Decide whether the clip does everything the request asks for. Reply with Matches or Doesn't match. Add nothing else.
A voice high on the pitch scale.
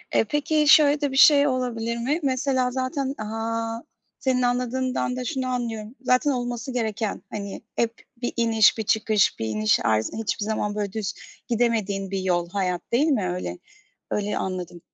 Matches